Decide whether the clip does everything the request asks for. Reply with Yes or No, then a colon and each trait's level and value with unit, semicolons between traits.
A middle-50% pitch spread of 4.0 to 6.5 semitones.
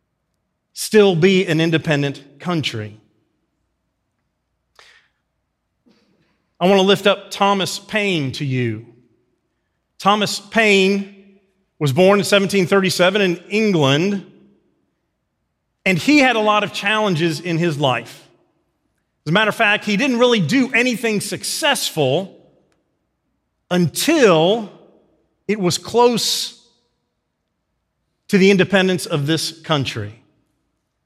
Yes: average, 4.9 semitones